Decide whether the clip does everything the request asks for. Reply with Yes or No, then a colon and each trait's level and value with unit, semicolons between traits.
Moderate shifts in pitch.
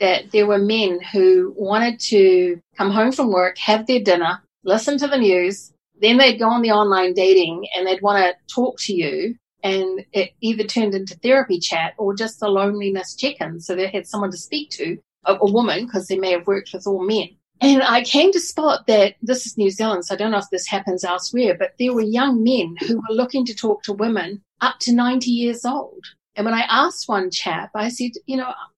Yes: average, 4.1 semitones